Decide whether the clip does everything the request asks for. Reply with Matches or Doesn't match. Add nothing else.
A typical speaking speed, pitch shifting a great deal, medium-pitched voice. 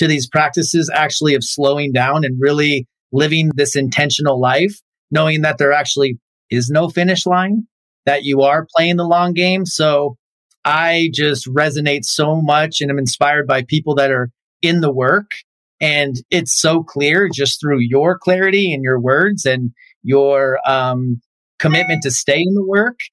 Doesn't match